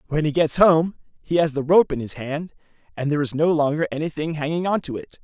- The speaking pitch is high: No, medium, 155 Hz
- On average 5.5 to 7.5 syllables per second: Yes, 6.1 syllables/s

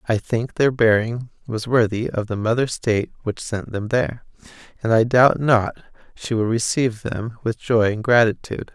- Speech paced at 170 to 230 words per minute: Yes, average, 180 wpm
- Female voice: No, male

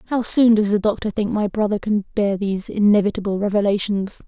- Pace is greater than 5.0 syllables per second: Yes, 5.6 syllables/s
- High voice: Yes, high, 205 Hz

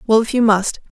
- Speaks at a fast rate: Yes, fast, 245 wpm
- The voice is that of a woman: Yes, female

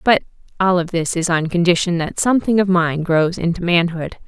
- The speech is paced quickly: No, average, 195 wpm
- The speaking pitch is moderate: Yes, medium, 175 Hz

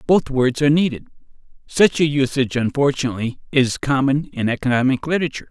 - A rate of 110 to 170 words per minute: Yes, average, 140 wpm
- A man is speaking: Yes, male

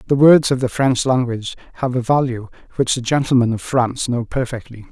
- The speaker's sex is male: Yes, male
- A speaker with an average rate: Yes, average, 195 wpm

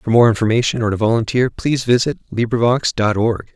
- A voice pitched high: No, low, 115 Hz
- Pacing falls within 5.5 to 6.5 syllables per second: Yes, 6.0 syllables/s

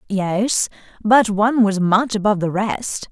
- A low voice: No, high, 210 Hz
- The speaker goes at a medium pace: Yes, average, 155 wpm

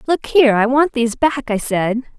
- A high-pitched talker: Yes, very high, 250 Hz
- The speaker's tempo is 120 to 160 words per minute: No, fast, 220 wpm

